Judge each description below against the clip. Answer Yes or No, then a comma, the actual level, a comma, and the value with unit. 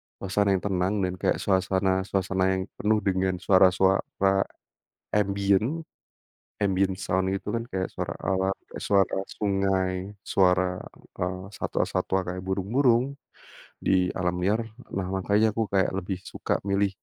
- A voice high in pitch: No, very low, 95 Hz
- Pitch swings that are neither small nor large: No, narrow, 1.2 semitones